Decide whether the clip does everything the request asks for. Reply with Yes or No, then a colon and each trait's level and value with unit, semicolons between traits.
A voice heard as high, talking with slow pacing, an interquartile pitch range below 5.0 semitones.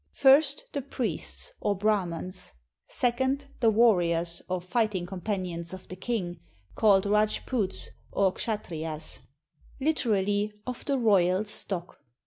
Yes: high, 205 Hz; slow, 115 wpm; average, 4.6 semitones